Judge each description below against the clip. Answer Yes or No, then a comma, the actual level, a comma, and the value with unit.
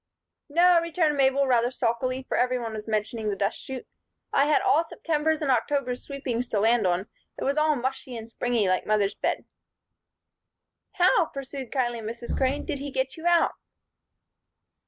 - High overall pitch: Yes, very high, 260 Hz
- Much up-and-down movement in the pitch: No, average, 3.9 semitones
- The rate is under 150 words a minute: No, average, 170 wpm